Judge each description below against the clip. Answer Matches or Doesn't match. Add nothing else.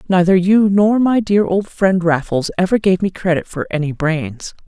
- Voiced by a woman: Matches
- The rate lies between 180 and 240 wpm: Matches